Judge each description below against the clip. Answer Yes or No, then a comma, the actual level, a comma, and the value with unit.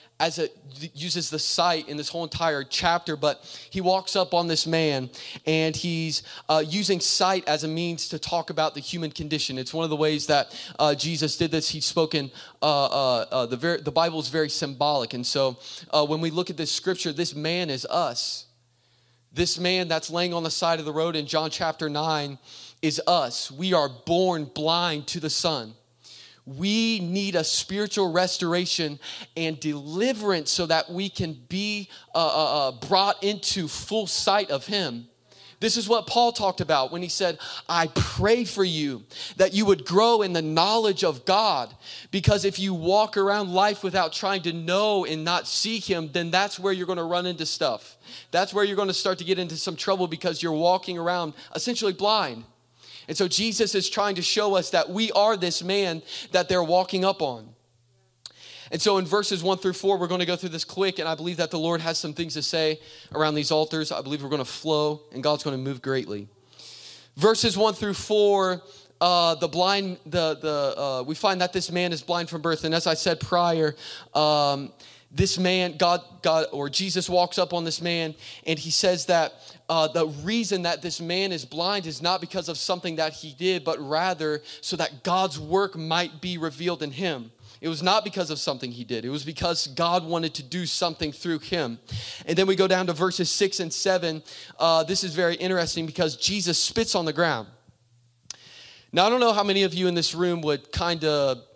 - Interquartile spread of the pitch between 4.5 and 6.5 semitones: No, average, 3.5 semitones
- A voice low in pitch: No, medium, 170 Hz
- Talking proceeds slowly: No, fast, 205 wpm